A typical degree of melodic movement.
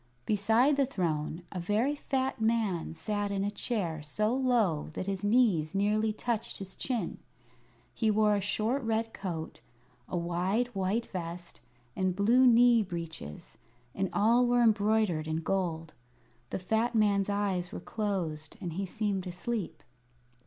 Yes: average, 4.2 semitones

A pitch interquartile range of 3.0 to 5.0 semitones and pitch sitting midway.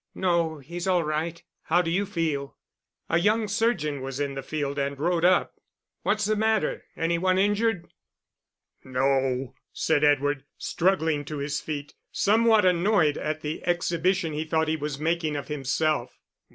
Yes: average, 4.1 semitones; medium, 160 Hz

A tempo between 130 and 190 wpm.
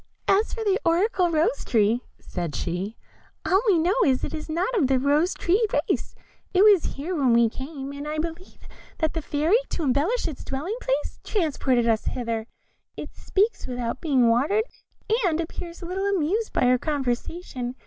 Yes: average, 180 wpm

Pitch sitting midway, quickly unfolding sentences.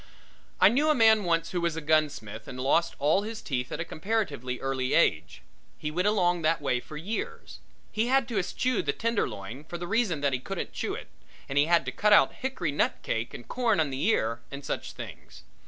Yes: medium, 165 Hz; fast, 220 wpm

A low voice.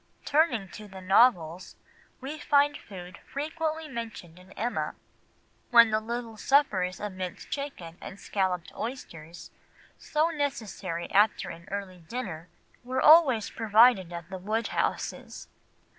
No: high, 215 Hz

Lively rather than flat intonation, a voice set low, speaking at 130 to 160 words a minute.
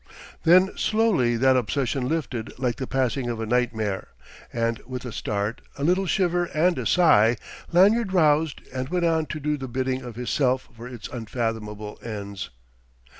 No: wide, 5.7 semitones; low, 130 Hz; average, 170 wpm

